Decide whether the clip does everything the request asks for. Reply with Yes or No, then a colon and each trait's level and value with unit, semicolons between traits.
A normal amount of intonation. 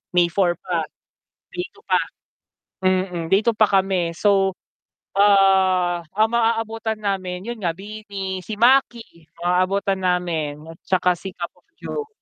Yes: average, 3.2 semitones